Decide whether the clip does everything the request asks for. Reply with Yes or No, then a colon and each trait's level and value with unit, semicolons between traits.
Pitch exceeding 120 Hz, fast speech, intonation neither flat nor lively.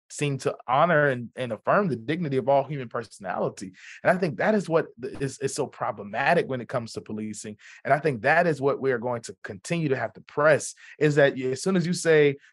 Yes: medium, 140 Hz; fast, 235 wpm; average, 3.7 semitones